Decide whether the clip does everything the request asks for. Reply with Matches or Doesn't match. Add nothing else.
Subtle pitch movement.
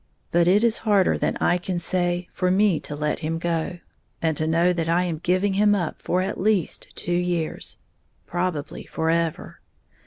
Matches